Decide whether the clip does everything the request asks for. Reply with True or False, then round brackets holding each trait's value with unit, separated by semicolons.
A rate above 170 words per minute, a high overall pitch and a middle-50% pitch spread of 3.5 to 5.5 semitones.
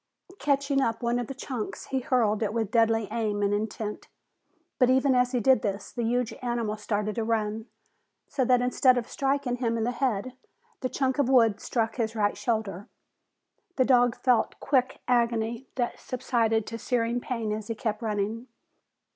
False (180 wpm; 235 Hz; 2.4 semitones)